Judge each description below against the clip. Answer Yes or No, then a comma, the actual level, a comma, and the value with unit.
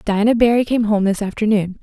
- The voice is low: No, high, 215 Hz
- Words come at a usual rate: Yes, average, 195 wpm